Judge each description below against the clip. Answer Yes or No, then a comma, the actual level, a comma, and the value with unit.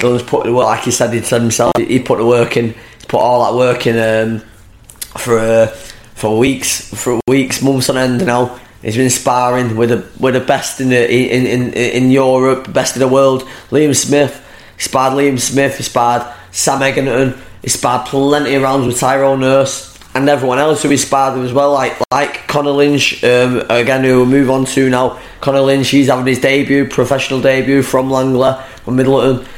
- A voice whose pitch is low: Yes, low, 130 Hz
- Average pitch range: No, narrow, 2.0 semitones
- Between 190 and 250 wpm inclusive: Yes, average, 195 wpm